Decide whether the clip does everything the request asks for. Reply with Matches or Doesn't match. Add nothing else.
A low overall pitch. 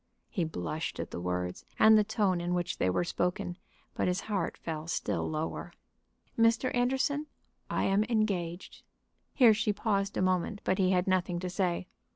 Doesn't match